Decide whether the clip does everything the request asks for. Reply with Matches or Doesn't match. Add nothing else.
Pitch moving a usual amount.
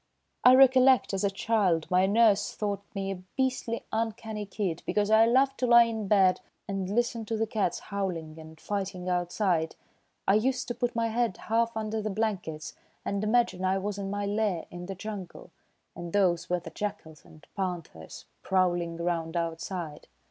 Matches